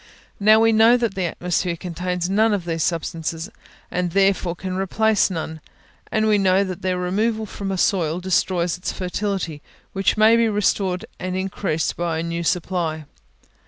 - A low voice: No, medium, 185 Hz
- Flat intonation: No, average, 3.0 semitones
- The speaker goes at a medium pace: Yes, average, 165 wpm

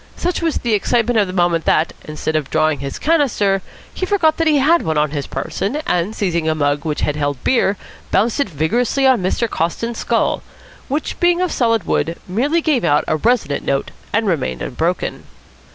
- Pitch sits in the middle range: No, high, 200 Hz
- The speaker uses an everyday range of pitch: No, wide, 8.9 semitones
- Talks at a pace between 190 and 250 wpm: Yes, average, 195 wpm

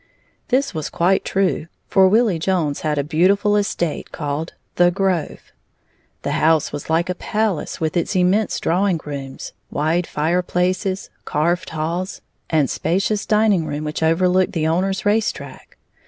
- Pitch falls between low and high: Yes, medium, 175 Hz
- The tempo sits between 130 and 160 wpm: Yes, average, 145 wpm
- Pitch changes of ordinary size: Yes, average, 3.4 semitones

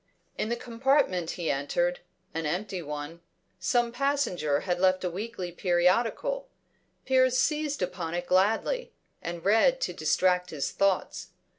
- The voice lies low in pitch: No, medium, 185 Hz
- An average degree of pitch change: No, wide, 5.9 semitones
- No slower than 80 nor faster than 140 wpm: Yes, slow, 135 wpm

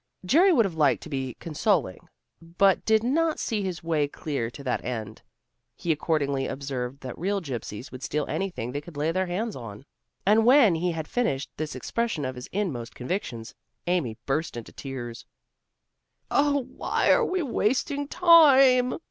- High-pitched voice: No, medium, 165 Hz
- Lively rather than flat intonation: Yes, wide, 9.0 semitones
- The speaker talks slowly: No, average, 165 wpm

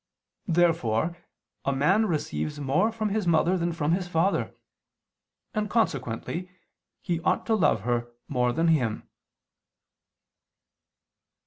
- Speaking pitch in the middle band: Yes, medium, 165 Hz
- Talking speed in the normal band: No, slow, 115 wpm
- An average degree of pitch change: No, wide, 6.3 semitones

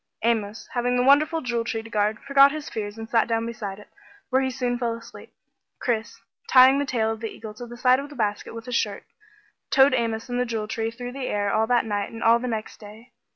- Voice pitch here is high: Yes, high, 230 Hz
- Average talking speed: No, fast, 245 wpm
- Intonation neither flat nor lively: No, narrow, 2.3 semitones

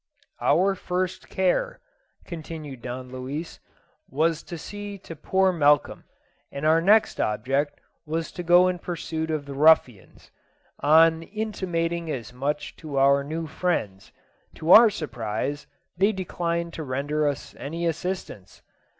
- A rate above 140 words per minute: No, slow, 135 wpm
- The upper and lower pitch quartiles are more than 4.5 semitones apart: No, average, 3.9 semitones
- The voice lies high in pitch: No, medium, 160 Hz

